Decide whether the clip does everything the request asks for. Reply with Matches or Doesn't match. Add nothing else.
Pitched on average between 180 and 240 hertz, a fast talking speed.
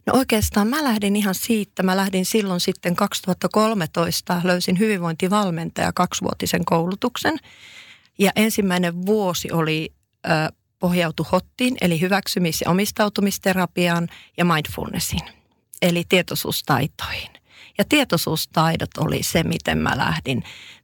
Doesn't match